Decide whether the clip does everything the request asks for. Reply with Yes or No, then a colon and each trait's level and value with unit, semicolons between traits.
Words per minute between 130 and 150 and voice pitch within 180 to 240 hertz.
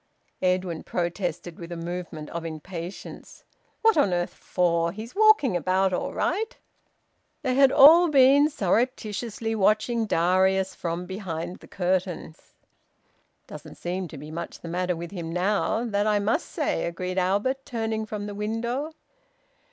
Yes: average, 145 wpm; high, 190 Hz